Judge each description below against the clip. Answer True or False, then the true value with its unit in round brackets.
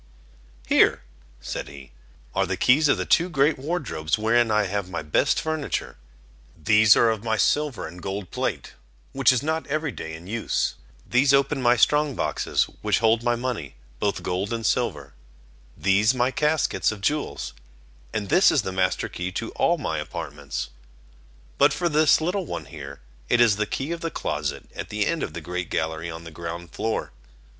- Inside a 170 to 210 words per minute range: True (185 wpm)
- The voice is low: True (110 Hz)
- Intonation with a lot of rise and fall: True (8.0 semitones)